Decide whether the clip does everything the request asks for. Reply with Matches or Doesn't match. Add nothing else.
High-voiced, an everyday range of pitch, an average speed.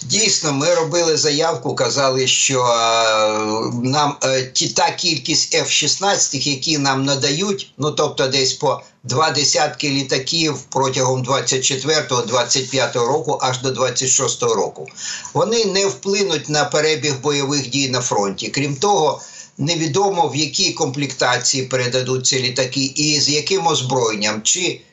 Doesn't match